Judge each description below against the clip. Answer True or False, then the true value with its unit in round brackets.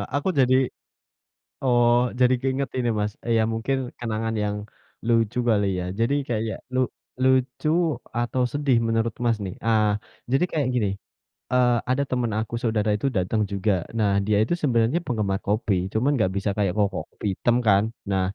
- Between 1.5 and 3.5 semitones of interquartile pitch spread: True (3.1 semitones)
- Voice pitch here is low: True (115 Hz)